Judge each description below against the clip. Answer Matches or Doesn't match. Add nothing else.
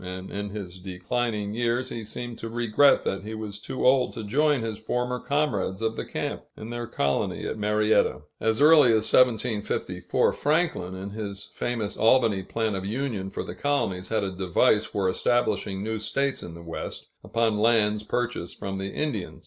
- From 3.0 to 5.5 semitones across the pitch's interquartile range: Matches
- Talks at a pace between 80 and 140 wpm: Doesn't match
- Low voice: Matches